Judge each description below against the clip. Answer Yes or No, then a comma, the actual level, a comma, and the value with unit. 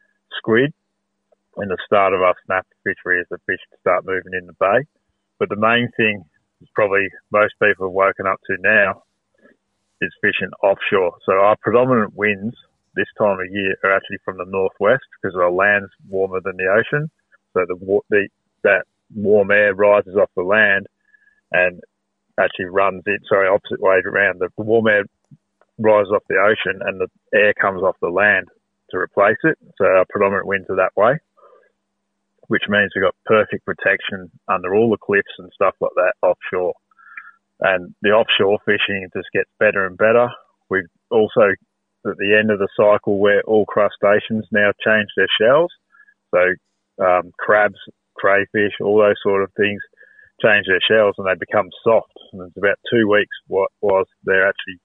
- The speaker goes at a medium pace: Yes, average, 175 wpm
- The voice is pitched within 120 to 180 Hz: No, low, 105 Hz